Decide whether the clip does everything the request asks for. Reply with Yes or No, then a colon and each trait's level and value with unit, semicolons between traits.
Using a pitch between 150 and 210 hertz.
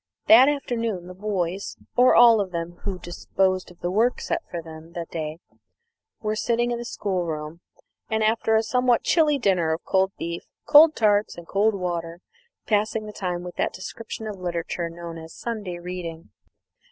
Yes: high, 190 Hz